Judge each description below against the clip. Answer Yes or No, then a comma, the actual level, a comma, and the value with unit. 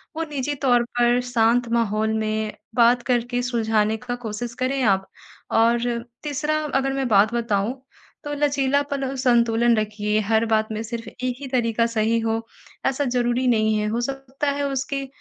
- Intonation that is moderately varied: Yes, average, 3.2 semitones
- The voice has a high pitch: Yes, high, 240 Hz